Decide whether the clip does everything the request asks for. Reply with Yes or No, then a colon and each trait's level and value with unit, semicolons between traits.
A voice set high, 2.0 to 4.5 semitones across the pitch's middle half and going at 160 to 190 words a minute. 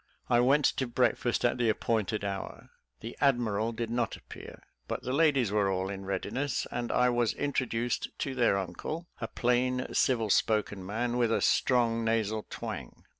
No: low, 115 Hz; average, 2.7 semitones; average, 170 wpm